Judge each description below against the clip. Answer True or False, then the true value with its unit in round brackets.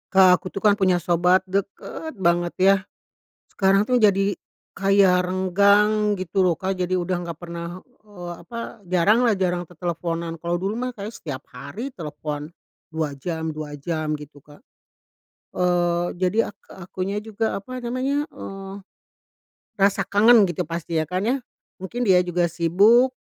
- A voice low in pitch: False (185 Hz)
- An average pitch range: True (3.0 semitones)